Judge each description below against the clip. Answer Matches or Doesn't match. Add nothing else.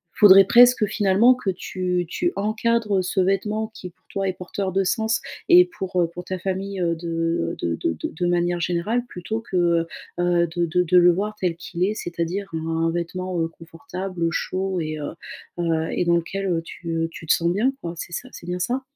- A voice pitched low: Doesn't match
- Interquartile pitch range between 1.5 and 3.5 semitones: Matches